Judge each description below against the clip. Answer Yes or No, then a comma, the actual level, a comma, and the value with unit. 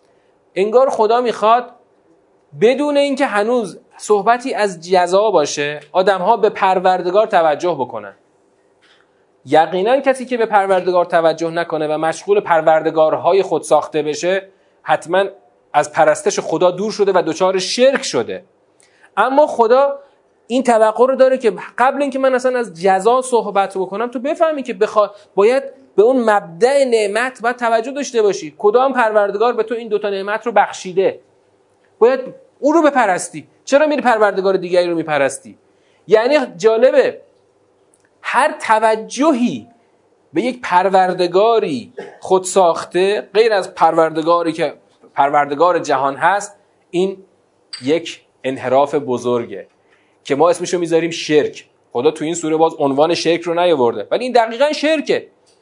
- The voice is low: No, high, 205 Hz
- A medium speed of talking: Yes, average, 135 wpm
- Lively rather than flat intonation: Yes, wide, 6.8 semitones